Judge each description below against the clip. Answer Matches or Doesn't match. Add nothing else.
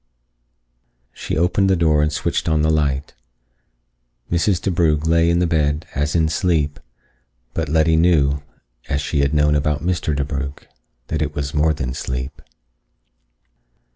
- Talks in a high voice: Doesn't match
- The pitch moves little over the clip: Matches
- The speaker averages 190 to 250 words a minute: Doesn't match